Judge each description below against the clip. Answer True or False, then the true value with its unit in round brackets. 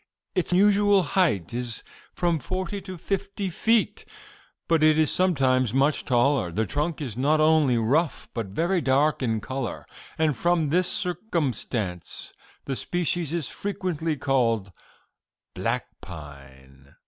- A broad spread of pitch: True (6.8 semitones)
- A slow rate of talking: True (130 wpm)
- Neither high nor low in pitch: True (150 Hz)